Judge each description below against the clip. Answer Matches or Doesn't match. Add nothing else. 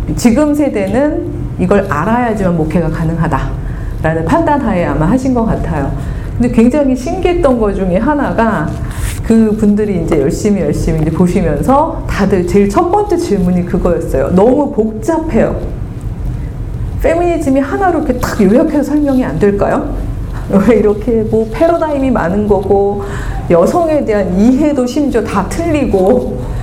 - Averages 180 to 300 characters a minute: Doesn't match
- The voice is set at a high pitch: Matches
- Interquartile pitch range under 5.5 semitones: Doesn't match